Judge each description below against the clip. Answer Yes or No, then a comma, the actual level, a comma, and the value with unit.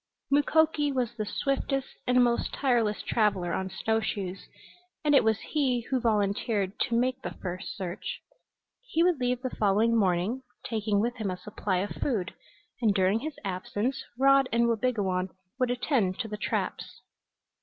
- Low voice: No, high, 225 Hz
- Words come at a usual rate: Yes, average, 160 wpm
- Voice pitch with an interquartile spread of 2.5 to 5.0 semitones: Yes, average, 4.4 semitones